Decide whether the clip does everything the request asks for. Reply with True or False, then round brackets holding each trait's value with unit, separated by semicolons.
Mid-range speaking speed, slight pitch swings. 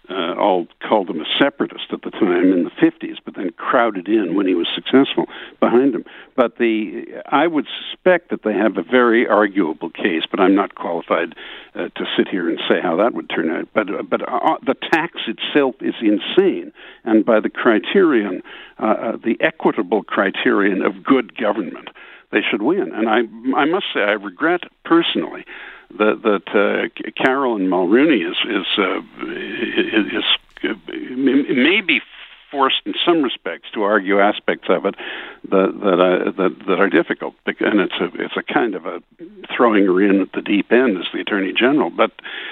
True (185 wpm; 2.2 semitones)